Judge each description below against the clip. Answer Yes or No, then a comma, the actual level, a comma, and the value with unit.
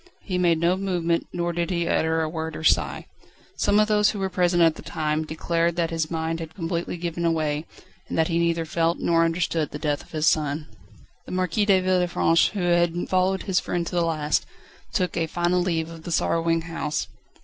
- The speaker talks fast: Yes, fast, 210 wpm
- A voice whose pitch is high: No, medium, 170 Hz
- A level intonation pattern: Yes, narrow, 1.7 semitones